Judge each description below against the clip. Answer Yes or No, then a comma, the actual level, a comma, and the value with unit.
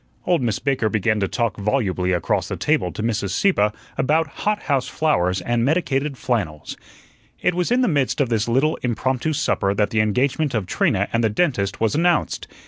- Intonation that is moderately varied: No, wide, 6.1 semitones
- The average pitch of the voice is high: No, low, 120 Hz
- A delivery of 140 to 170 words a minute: No, average, 190 wpm